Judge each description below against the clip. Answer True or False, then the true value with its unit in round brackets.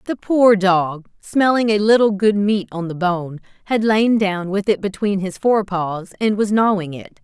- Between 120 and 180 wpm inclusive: False (200 wpm)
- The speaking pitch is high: True (200 Hz)